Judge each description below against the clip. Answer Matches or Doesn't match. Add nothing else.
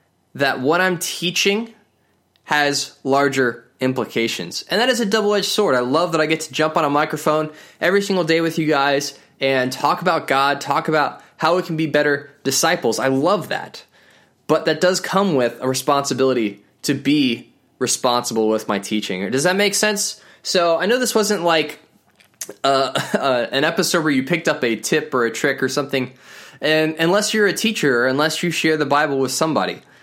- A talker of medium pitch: Matches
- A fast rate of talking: Doesn't match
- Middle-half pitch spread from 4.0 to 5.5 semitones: Matches